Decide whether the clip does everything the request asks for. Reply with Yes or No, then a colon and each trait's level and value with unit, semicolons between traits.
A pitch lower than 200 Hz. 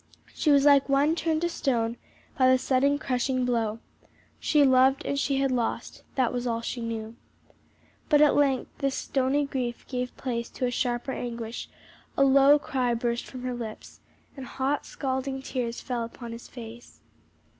No: very high, 255 Hz